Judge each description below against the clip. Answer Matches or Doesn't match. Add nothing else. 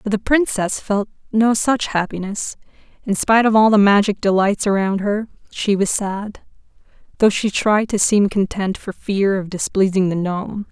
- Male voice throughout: Doesn't match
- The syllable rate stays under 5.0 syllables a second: Matches